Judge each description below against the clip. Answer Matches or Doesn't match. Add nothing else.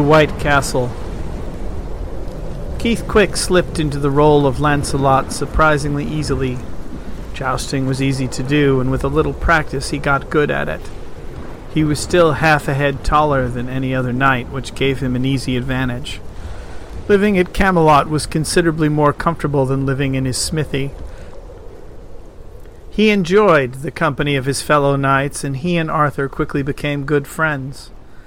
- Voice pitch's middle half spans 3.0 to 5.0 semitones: Doesn't match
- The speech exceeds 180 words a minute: Doesn't match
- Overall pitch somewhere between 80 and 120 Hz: Doesn't match